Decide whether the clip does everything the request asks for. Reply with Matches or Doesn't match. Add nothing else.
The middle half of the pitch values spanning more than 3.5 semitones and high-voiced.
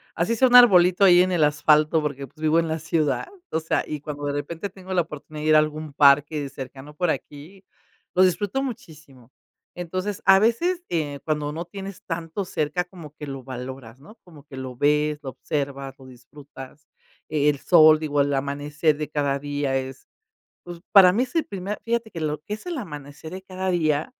Doesn't match